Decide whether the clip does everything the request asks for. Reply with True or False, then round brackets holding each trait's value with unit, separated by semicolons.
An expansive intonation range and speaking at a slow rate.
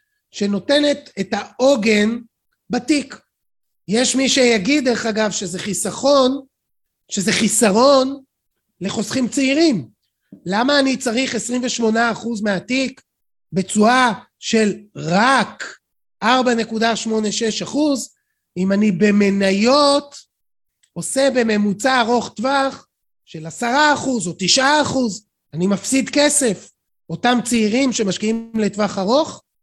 False (4.5 semitones; 85 wpm)